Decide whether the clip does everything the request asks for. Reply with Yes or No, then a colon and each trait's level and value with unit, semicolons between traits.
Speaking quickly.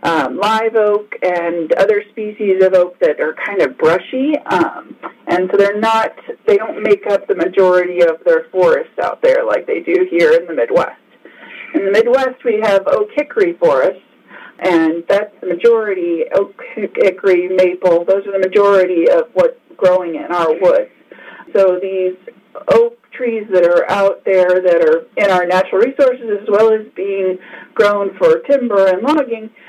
No: average, 170 wpm